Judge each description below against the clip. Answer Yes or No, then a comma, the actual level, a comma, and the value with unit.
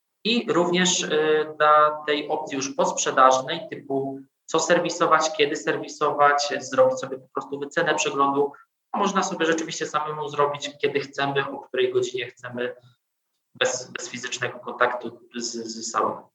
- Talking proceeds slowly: No, average, 130 wpm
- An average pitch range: Yes, average, 3.2 semitones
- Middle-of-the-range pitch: Yes, medium, 150 Hz